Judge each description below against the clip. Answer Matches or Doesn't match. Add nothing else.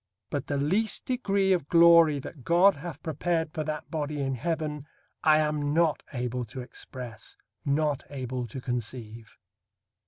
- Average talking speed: Matches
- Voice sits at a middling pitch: Matches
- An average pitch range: Matches